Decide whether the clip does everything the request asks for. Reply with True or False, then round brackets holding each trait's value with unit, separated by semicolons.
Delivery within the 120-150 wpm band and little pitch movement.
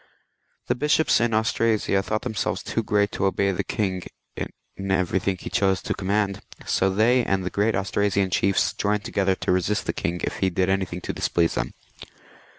False (190 wpm; 2.0 semitones)